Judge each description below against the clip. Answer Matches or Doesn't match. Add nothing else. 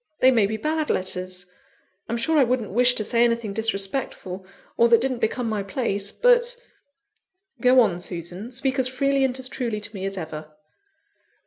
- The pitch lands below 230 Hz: Doesn't match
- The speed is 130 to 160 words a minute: Doesn't match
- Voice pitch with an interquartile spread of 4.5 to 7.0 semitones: Matches